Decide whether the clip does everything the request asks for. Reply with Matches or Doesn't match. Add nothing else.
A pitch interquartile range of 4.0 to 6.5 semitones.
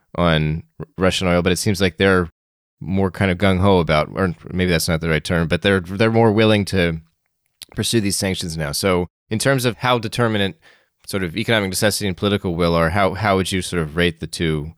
Doesn't match